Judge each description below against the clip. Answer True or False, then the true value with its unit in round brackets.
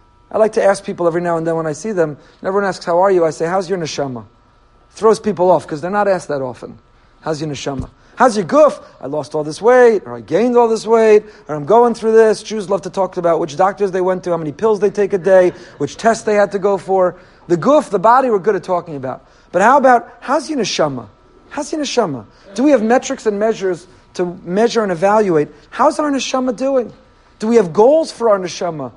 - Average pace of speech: False (245 wpm)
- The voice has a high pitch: True (195 Hz)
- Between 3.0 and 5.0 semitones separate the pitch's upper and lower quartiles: False (5.5 semitones)